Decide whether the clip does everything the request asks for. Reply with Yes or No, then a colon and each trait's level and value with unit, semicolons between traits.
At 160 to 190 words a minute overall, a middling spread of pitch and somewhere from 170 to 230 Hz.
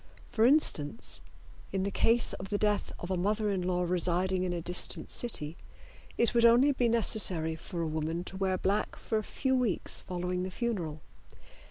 Yes: average, 185 wpm; average, 4.2 semitones; high, 190 Hz